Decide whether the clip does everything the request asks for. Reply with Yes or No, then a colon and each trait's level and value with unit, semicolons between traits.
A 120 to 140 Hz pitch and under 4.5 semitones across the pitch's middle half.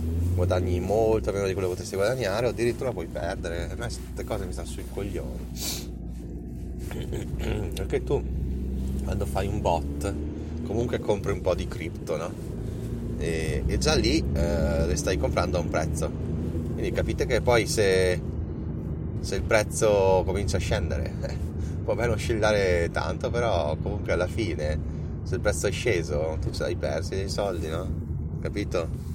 No: very low, 85 Hz; average, 4.1 semitones